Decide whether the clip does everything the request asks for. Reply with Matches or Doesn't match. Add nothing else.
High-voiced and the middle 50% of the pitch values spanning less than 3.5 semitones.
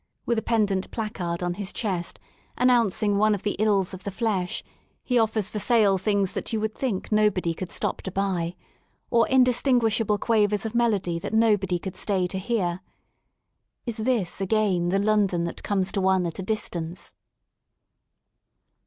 Matches